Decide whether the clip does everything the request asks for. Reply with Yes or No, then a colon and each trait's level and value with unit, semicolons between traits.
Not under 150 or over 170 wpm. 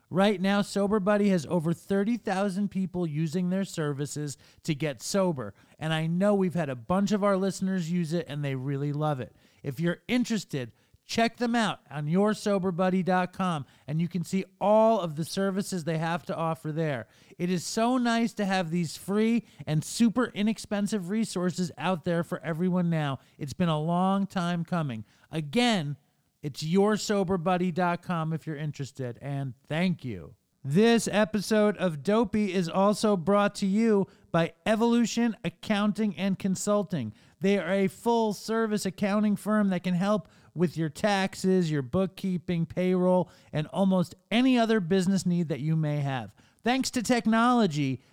Yes: average, 160 wpm